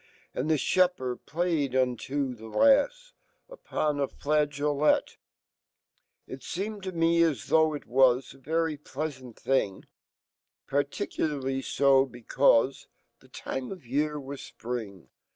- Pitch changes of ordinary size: Yes, average, 3.5 semitones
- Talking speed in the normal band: No, slow, 105 wpm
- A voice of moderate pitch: Yes, medium, 145 Hz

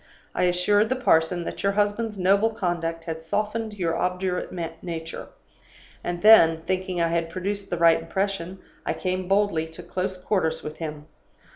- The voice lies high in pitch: No, medium, 180 Hz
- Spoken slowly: No, average, 160 wpm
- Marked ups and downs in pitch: No, average, 3.3 semitones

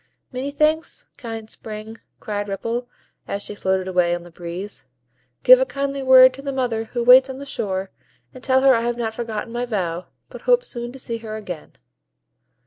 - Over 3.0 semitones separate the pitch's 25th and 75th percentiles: Yes, average, 4.3 semitones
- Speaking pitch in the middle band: No, high, 230 Hz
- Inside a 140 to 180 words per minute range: No, average, 195 wpm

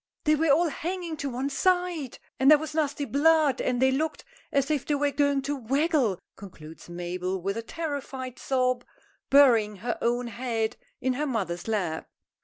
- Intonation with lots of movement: No, average, 4.7 semitones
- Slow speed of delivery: No, average, 175 wpm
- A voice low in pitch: No, very high, 270 Hz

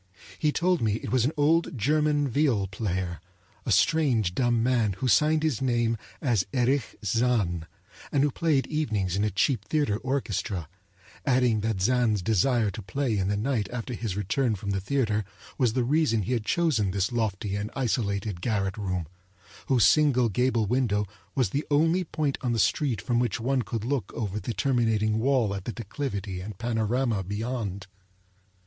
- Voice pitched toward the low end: Yes, low, 115 Hz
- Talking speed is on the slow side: No, average, 175 wpm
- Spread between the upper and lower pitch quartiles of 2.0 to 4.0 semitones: No, average, 4.6 semitones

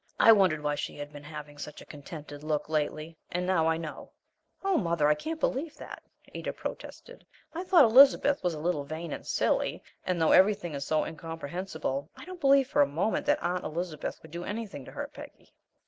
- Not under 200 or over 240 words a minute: Yes, fast, 205 wpm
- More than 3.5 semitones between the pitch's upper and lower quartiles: Yes, wide, 5.6 semitones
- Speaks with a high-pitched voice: No, medium, 165 Hz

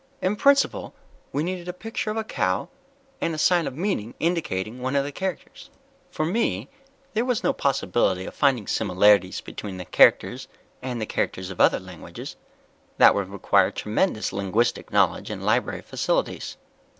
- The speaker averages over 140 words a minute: Yes, average, 160 wpm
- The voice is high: No, low, 130 Hz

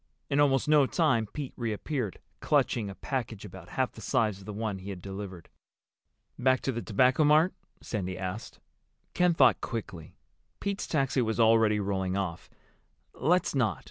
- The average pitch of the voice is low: Yes, low, 115 Hz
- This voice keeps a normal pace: Yes, average, 160 wpm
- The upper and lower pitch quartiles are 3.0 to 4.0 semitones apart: No, wide, 5.5 semitones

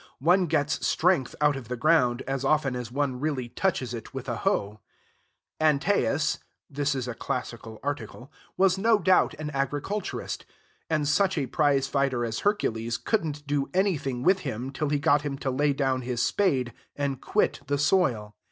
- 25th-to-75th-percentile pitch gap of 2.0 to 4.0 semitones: Yes, average, 3.5 semitones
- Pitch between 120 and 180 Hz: Yes, medium, 140 Hz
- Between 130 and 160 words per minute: No, average, 175 wpm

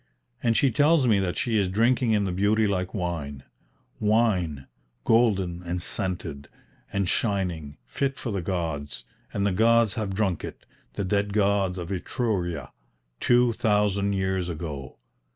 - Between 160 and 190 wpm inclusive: No, average, 150 wpm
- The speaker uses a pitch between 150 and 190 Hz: No, low, 100 Hz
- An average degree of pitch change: Yes, average, 3.9 semitones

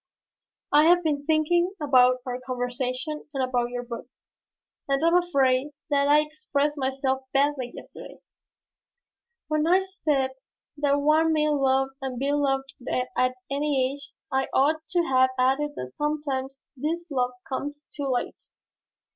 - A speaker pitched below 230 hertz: No, very high, 280 Hz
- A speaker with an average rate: Yes, average, 145 wpm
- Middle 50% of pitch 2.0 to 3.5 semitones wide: Yes, narrow, 2.6 semitones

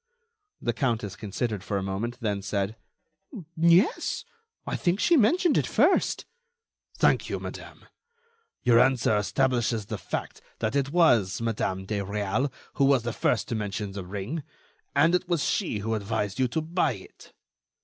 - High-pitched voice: No, low, 115 Hz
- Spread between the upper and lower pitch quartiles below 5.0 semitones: No, wide, 5.5 semitones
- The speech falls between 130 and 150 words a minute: No, average, 160 wpm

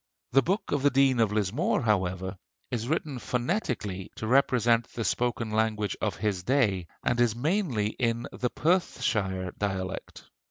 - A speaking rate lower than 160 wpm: Yes, average, 150 wpm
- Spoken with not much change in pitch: No, average, 4.1 semitones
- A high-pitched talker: No, low, 115 Hz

